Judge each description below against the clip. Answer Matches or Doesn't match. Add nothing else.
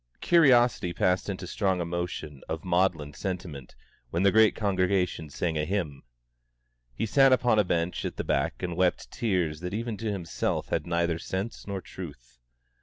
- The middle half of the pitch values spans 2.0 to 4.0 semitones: Matches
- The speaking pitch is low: Matches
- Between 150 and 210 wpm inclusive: Matches